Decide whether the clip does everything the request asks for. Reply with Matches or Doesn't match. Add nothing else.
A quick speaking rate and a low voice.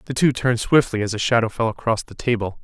Matches